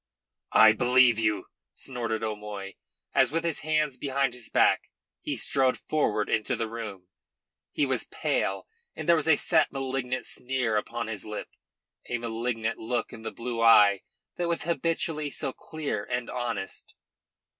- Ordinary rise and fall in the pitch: Yes, average, 3.9 semitones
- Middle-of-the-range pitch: No, low, 125 Hz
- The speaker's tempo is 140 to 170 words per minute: Yes, average, 155 wpm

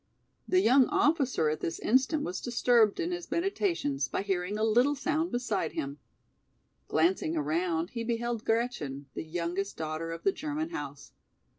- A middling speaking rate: Yes, average, 155 wpm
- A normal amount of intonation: No, wide, 8.4 semitones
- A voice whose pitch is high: Yes, high, 215 Hz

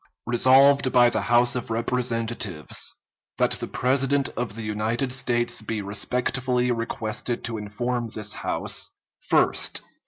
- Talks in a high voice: No, low, 120 Hz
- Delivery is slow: Yes, slow, 125 wpm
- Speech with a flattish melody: Yes, narrow, 2.1 semitones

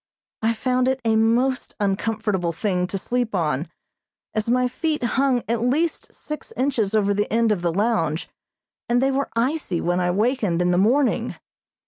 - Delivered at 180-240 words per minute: No, average, 170 wpm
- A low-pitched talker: No, high, 225 Hz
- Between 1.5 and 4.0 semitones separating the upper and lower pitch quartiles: No, average, 4.8 semitones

